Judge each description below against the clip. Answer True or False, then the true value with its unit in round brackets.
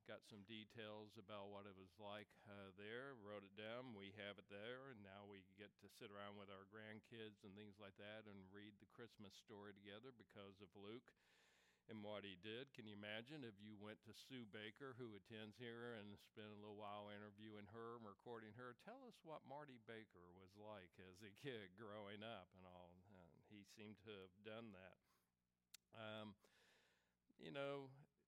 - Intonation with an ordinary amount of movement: False (2.0 semitones)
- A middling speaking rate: True (190 wpm)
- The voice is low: True (105 Hz)